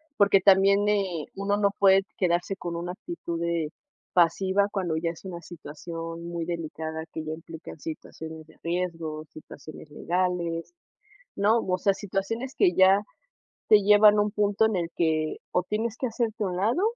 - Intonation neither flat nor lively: Yes, average, 3.5 semitones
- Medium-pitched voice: Yes, medium, 180 Hz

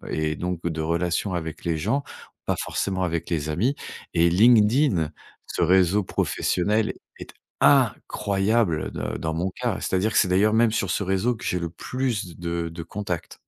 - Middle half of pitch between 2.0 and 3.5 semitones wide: No, average, 4.1 semitones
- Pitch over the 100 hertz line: No, very low, 90 Hz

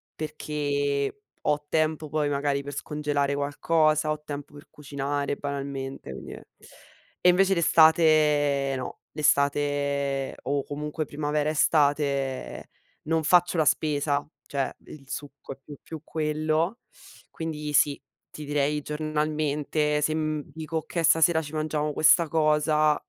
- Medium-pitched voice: Yes, medium, 150 Hz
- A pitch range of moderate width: No, narrow, 1.5 semitones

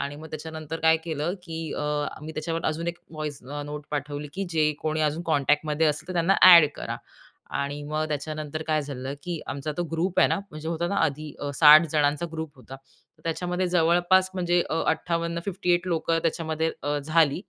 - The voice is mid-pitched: Yes, medium, 160 Hz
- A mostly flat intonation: Yes, narrow, 2.2 semitones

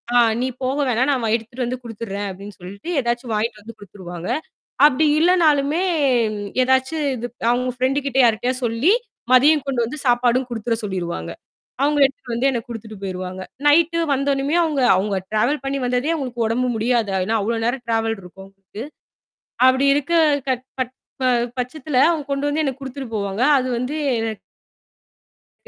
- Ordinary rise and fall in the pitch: Yes, average, 3.8 semitones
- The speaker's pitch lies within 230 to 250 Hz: Yes, high, 245 Hz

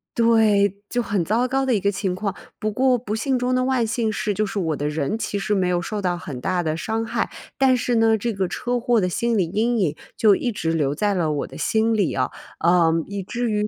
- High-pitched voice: Yes, high, 210 Hz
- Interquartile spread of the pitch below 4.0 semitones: No, average, 4.3 semitones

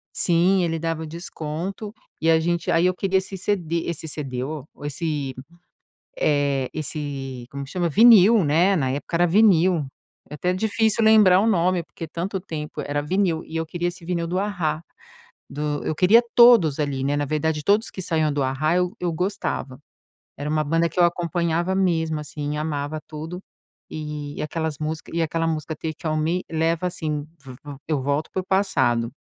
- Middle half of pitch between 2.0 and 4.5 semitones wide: Yes, average, 3.3 semitones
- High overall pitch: No, medium, 160 Hz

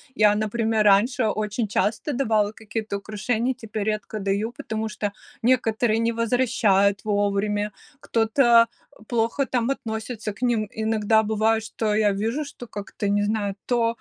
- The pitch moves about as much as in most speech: No, narrow, 1.9 semitones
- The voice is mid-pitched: No, high, 220 Hz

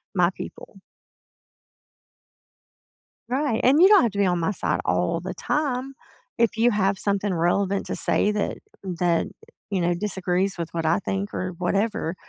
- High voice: Yes, high, 200 Hz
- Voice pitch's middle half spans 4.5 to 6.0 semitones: No, average, 4.1 semitones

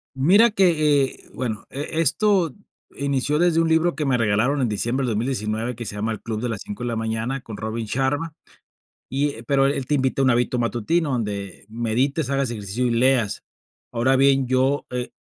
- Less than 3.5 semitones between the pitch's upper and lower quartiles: No, average, 3.9 semitones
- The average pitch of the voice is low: Yes, low, 130 Hz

